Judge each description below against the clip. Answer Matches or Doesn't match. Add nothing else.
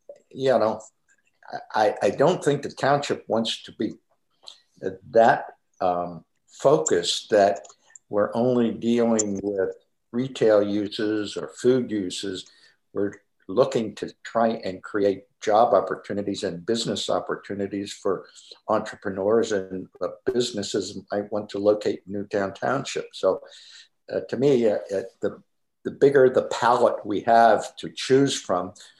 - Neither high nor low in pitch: Doesn't match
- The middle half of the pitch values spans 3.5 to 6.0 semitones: Matches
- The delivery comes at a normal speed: Doesn't match